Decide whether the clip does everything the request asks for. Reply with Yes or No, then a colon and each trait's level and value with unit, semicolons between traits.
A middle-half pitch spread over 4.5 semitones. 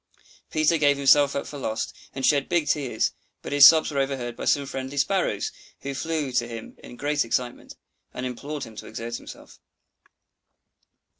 No: average, 2.9 semitones